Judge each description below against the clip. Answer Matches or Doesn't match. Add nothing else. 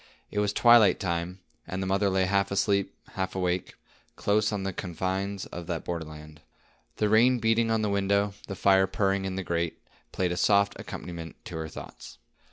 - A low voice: Matches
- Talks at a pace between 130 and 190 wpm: Matches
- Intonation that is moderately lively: Doesn't match